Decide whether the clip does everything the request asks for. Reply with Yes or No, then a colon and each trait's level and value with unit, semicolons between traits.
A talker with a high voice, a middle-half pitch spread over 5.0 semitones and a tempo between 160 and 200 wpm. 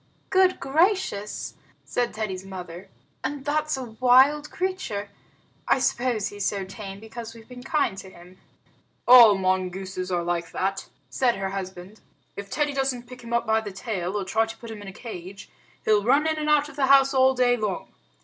Yes: high, 225 Hz; wide, 5.4 semitones; average, 190 wpm